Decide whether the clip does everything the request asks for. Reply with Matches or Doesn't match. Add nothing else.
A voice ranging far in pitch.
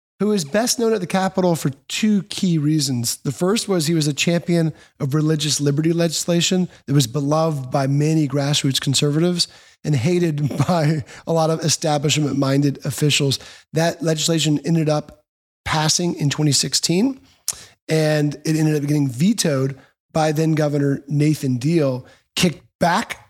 Doesn't match